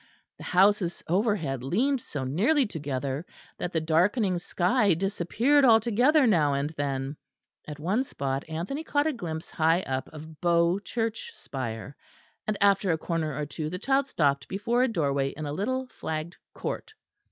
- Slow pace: No, average, 160 wpm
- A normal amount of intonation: No, wide, 7.1 semitones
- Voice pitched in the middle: Yes, medium, 175 Hz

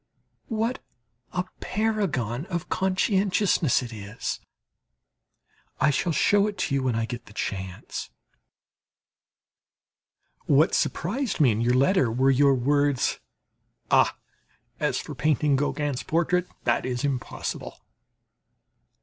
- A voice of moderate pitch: Yes, medium, 145 Hz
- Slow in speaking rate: Yes, slow, 115 wpm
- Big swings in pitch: Yes, wide, 6.9 semitones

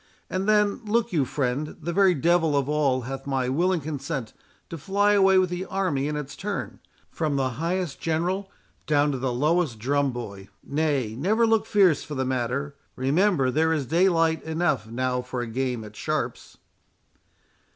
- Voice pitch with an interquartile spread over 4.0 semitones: Yes, average, 5.3 semitones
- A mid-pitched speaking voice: Yes, medium, 150 Hz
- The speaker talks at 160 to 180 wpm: Yes, average, 170 wpm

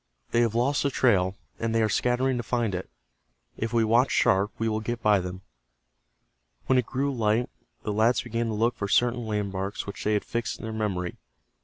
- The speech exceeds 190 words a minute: Yes, fast, 205 wpm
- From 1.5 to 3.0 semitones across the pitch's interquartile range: Yes, narrow, 2.5 semitones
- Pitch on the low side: Yes, low, 110 Hz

